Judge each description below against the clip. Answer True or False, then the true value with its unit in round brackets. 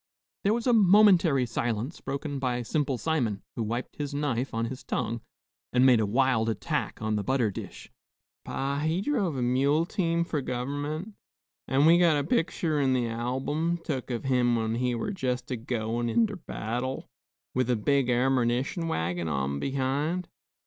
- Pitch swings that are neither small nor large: True (4.7 semitones)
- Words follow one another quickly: False (170 wpm)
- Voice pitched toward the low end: True (130 Hz)